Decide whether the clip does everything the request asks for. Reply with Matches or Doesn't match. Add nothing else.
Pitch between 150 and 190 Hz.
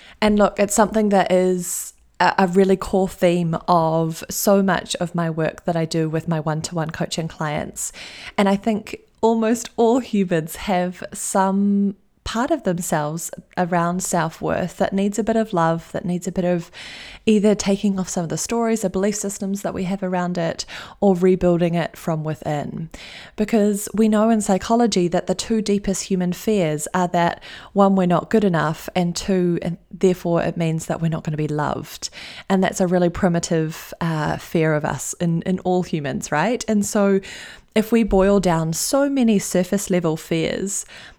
Matches